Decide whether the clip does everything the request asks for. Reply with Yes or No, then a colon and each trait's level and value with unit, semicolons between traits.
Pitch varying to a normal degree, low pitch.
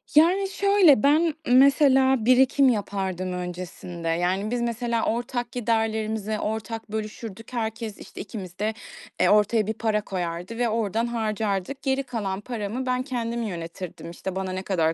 No: average, 4.1 semitones; high, 220 Hz